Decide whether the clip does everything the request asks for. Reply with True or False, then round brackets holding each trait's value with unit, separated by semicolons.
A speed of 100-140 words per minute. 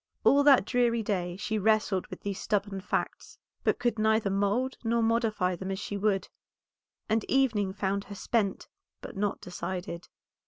False (160 wpm)